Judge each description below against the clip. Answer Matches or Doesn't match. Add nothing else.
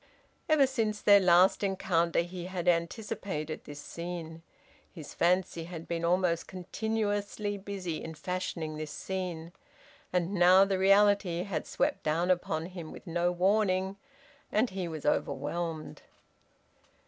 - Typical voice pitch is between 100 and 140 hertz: Doesn't match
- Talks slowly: Matches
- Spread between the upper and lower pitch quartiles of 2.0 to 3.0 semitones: Matches